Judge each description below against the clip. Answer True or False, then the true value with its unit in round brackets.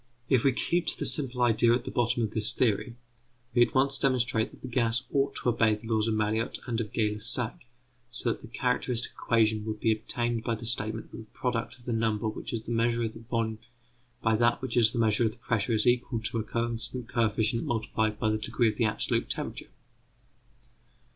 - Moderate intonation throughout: False (1.7 semitones)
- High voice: False (115 Hz)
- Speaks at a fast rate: True (220 wpm)